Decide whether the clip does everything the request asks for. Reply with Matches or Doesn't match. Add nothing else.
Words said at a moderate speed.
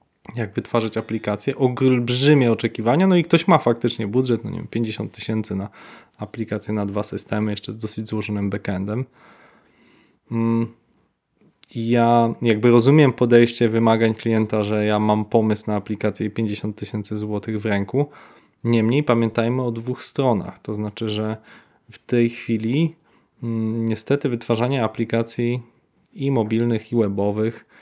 Matches